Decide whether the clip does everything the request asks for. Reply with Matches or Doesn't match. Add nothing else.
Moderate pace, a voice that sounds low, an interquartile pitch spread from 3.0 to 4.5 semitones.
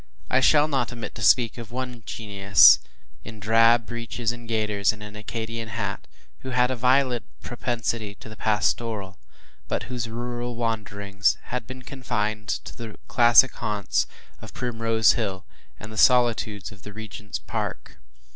Doesn't match